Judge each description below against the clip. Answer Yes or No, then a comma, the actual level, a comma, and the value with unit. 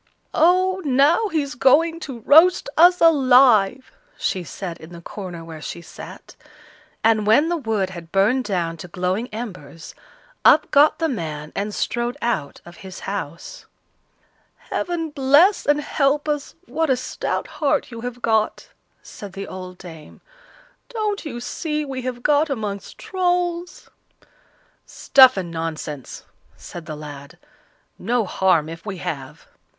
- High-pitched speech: Yes, high, 235 Hz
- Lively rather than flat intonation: Yes, wide, 8.7 semitones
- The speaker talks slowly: No, average, 145 wpm